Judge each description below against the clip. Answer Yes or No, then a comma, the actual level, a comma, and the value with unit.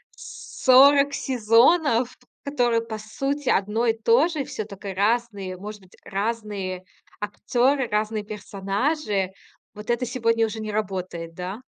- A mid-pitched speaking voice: No, high, 220 Hz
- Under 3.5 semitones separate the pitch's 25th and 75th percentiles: No, average, 3.8 semitones